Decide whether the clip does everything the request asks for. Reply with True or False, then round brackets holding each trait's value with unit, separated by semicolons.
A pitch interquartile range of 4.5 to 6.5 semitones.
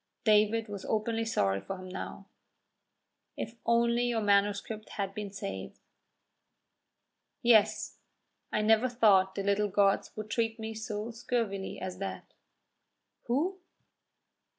False (2.4 semitones)